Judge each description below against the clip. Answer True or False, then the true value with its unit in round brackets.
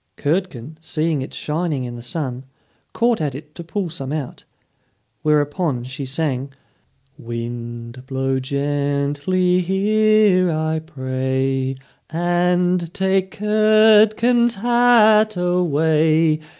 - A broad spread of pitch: True (5.7 semitones)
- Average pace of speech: False (100 wpm)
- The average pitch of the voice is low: False (160 Hz)